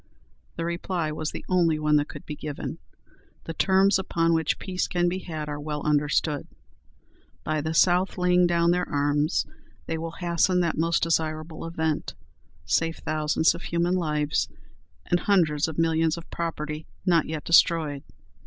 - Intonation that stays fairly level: Yes, narrow, 2.1 semitones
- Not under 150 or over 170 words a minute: Yes, average, 160 wpm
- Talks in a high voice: No, medium, 165 Hz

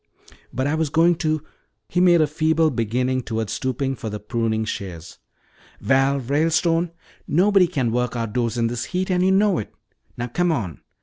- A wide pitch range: Yes, wide, 6.0 semitones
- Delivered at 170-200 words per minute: Yes, average, 180 wpm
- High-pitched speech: No, low, 135 Hz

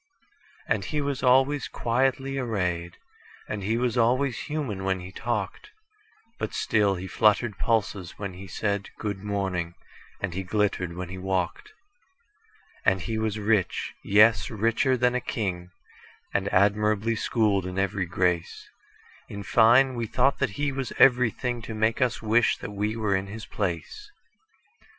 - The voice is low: Yes, low, 110 Hz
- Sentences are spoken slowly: Yes, slow, 130 wpm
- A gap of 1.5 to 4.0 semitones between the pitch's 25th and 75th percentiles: No, average, 4.5 semitones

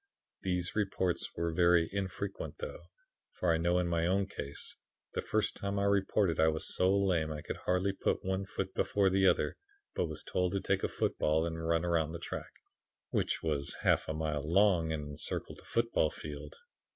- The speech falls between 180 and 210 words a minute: Yes, average, 190 wpm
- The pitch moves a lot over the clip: No, average, 3.3 semitones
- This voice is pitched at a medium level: No, very low, 85 Hz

